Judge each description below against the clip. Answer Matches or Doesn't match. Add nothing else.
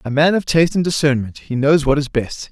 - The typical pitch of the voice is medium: Matches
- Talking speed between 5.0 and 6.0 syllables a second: Matches